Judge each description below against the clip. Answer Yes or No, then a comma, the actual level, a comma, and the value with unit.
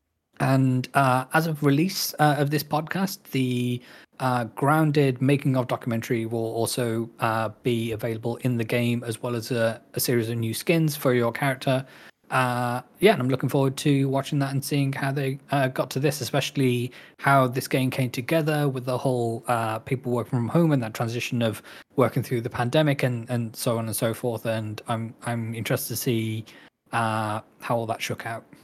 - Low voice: Yes, low, 125 Hz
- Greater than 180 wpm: Yes, average, 195 wpm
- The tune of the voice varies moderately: Yes, average, 3.0 semitones